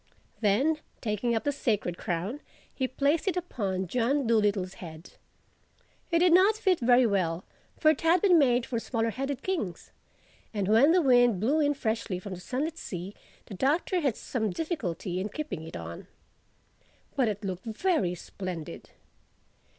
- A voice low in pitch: No, high, 235 Hz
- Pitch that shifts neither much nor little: No, wide, 7.6 semitones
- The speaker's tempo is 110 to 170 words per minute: Yes, average, 160 wpm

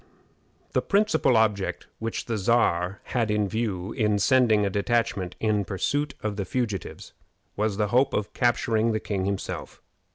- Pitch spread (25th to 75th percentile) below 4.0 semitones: Yes, average, 2.9 semitones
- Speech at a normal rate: Yes, average, 155 wpm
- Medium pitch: No, low, 110 Hz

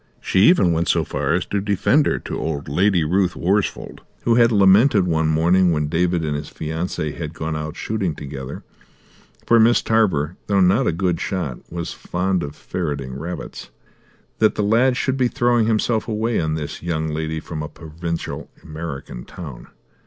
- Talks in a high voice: No, very low, 85 Hz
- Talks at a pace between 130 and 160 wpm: No, average, 175 wpm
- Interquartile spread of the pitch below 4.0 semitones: No, average, 4.8 semitones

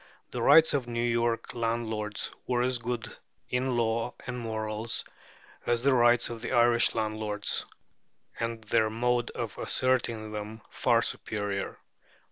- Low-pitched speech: Yes, low, 115 Hz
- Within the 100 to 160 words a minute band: Yes, average, 140 wpm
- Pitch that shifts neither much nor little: No, narrow, 1.7 semitones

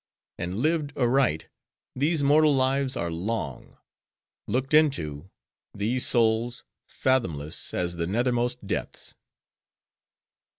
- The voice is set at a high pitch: No, low, 120 Hz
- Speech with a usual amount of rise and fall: No, wide, 7.1 semitones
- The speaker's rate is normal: No, slow, 95 wpm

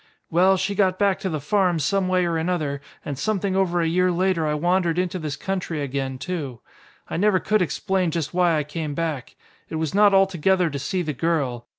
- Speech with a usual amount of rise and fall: Yes, average, 3.8 semitones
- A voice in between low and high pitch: Yes, medium, 175 Hz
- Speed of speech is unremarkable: No, fast, 210 wpm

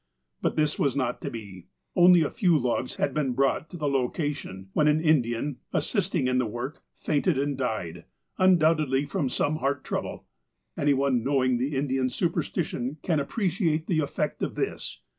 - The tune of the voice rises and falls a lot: No, average, 3.5 semitones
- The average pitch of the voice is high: No, medium, 140 Hz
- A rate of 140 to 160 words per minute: No, average, 170 wpm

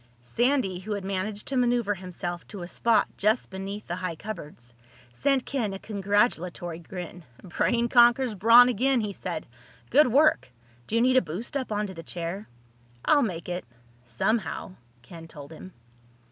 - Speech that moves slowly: No, average, 160 wpm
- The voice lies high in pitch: Yes, high, 200 Hz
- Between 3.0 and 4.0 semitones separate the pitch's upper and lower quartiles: No, average, 5.3 semitones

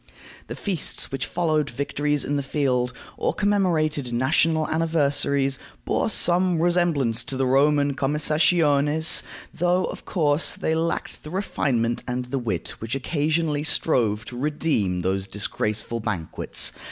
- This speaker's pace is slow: Yes, slow, 130 wpm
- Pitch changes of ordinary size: Yes, average, 4.2 semitones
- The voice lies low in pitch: No, medium, 145 Hz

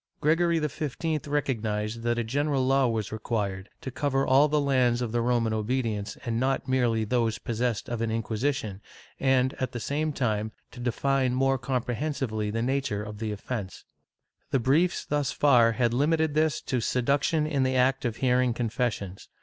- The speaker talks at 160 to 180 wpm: Yes, average, 170 wpm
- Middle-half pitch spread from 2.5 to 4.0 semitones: Yes, average, 3.4 semitones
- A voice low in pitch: Yes, low, 125 Hz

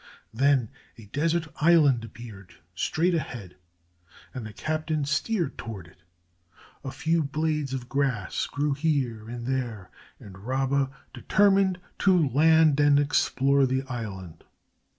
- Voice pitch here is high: No, low, 135 Hz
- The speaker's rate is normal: No, slow, 125 wpm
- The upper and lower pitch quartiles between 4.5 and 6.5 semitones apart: Yes, average, 5.2 semitones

